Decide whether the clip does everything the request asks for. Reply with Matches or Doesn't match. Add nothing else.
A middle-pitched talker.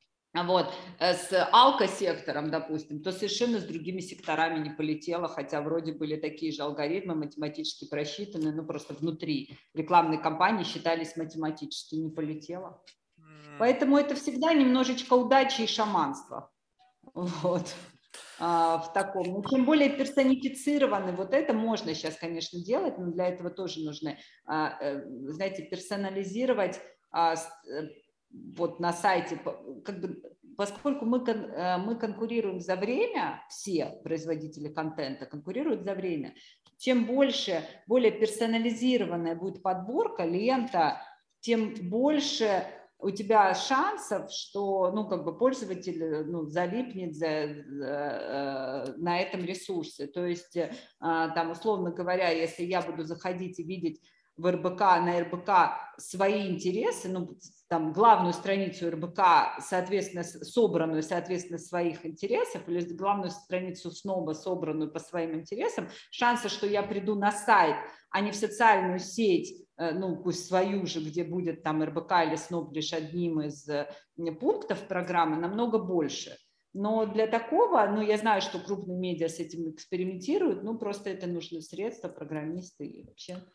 Matches